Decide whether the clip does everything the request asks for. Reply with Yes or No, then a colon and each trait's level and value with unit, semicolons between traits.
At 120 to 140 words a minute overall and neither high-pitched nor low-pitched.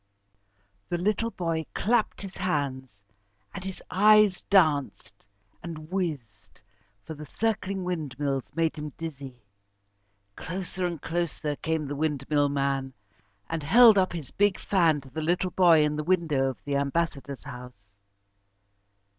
Yes: slow, 135 wpm; medium, 160 Hz